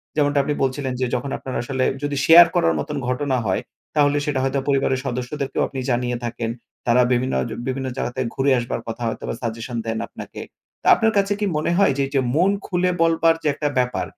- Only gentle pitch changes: No, average, 3.1 semitones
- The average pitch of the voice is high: No, low, 135 Hz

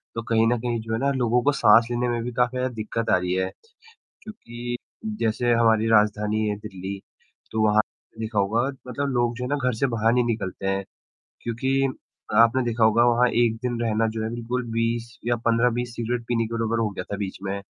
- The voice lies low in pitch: Yes, low, 115 Hz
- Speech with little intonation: Yes, narrow, 1.9 semitones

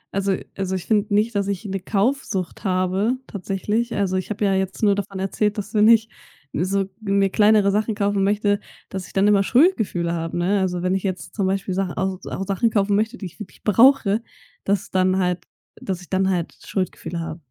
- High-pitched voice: Yes, high, 195 Hz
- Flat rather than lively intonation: Yes, narrow, 1.9 semitones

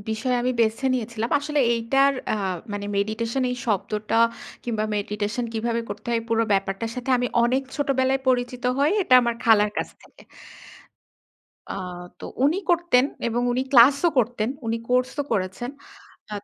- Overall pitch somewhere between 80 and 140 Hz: No, high, 235 Hz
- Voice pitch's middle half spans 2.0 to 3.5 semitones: Yes, average, 2.8 semitones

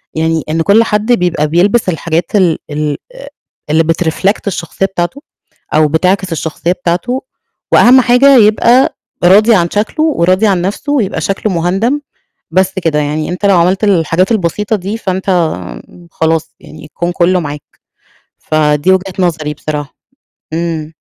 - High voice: No, medium, 180 Hz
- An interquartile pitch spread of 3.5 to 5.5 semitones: Yes, average, 4.2 semitones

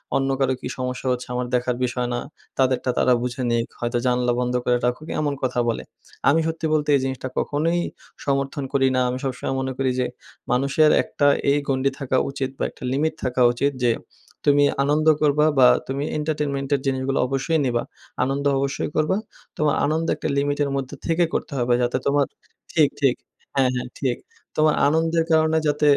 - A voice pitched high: No, low, 135 Hz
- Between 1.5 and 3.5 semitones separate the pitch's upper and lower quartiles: Yes, average, 2.8 semitones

